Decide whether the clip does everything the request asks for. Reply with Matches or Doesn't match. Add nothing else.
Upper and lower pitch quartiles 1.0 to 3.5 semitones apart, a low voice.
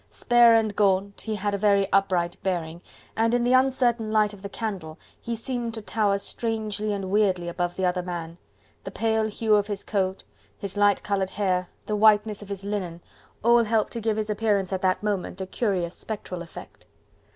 Doesn't match